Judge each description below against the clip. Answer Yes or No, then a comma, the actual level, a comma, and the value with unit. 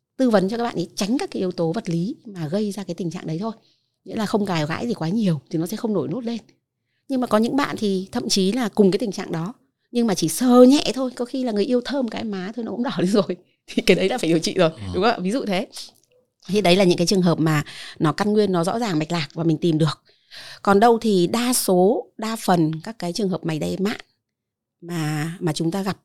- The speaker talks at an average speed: No, fast, 280 wpm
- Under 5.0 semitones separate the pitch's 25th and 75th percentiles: No, average, 5.3 semitones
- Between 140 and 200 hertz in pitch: Yes, high, 195 Hz